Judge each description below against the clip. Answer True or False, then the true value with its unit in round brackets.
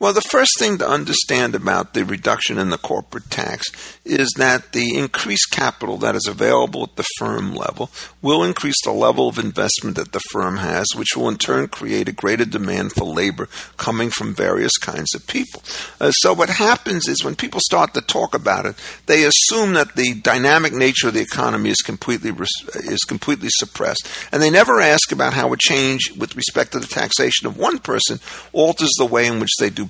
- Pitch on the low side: True (130 Hz)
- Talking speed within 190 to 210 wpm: True (205 wpm)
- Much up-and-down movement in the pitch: False (4.2 semitones)